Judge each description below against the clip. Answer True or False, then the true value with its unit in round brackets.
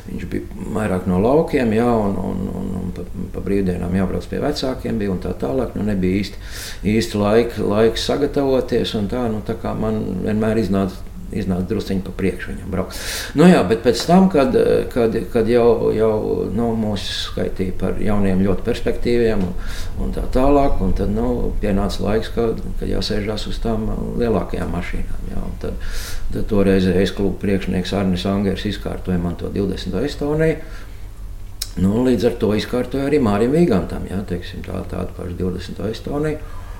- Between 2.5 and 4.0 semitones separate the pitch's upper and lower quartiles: True (3.1 semitones)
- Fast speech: False (150 wpm)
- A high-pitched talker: False (95 Hz)